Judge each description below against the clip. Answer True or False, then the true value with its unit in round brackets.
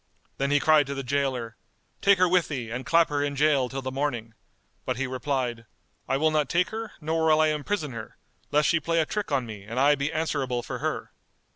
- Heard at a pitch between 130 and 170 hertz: True (140 Hz)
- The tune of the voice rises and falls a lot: False (3.4 semitones)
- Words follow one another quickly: True (230 wpm)